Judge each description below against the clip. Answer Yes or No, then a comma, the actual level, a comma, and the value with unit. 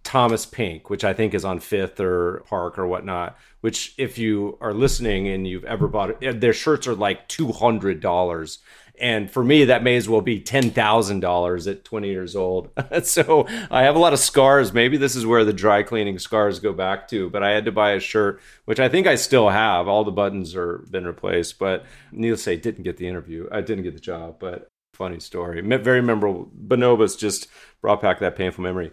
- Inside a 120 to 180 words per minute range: No, fast, 205 wpm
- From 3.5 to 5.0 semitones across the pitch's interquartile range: Yes, average, 4.4 semitones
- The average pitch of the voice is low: Yes, low, 105 Hz